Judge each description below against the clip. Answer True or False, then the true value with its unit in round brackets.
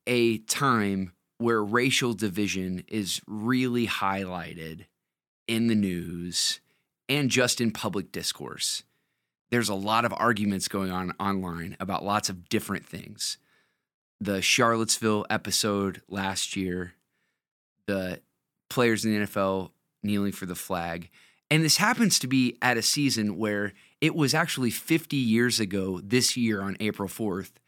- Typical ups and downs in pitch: True (4.1 semitones)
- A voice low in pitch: True (105 Hz)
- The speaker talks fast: False (135 wpm)